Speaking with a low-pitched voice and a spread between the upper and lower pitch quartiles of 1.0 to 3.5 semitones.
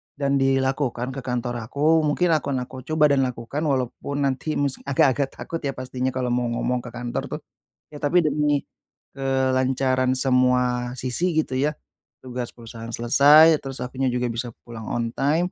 Yes: low, 130 Hz; narrow, 2.4 semitones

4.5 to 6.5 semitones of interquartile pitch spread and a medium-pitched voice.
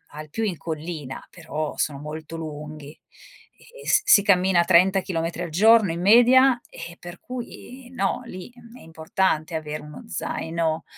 Yes: wide, 5.5 semitones; medium, 170 Hz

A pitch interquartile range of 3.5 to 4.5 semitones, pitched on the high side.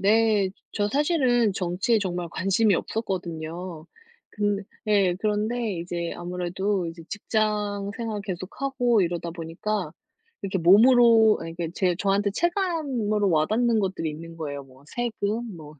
Yes: average, 4.2 semitones; high, 200 Hz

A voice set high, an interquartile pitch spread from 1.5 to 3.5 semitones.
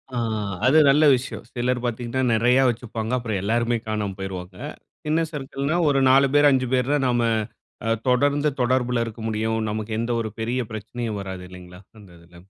No: low, 120 Hz; average, 3.2 semitones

